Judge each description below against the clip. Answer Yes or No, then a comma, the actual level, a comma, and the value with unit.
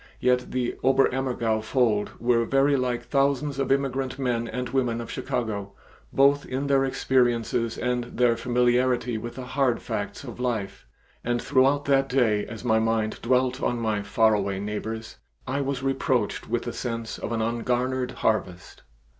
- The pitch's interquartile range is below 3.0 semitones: Yes, narrow, 2.6 semitones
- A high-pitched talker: No, low, 125 Hz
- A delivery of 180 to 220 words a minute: No, average, 165 wpm